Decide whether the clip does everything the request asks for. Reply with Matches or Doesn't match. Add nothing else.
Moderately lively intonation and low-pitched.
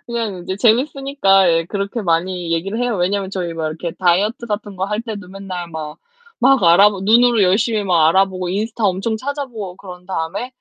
Doesn't match